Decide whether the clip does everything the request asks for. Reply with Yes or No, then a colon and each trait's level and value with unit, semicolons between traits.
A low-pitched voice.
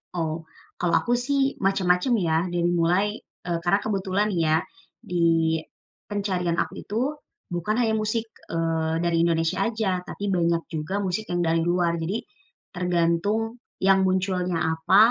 No: medium, 180 Hz